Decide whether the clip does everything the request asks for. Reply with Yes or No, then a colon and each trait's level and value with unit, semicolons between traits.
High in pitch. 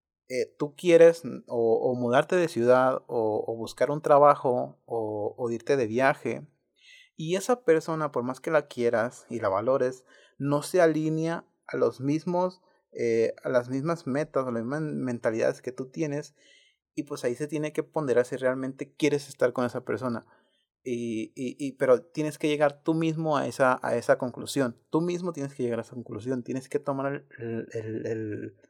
No: medium, 140 Hz